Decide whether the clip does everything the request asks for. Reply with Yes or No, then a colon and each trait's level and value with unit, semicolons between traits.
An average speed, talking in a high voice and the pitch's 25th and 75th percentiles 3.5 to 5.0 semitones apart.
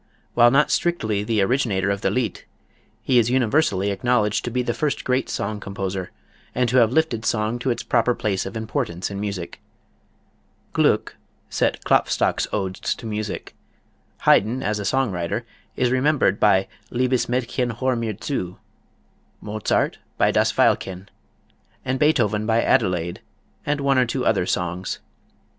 No: average, 150 wpm; low, 110 Hz; average, 4.3 semitones